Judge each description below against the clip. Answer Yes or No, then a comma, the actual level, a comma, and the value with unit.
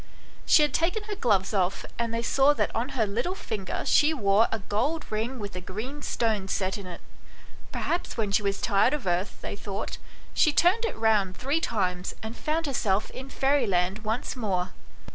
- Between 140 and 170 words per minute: No, average, 190 wpm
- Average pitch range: No, wide, 6.1 semitones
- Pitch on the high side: Yes, high, 220 Hz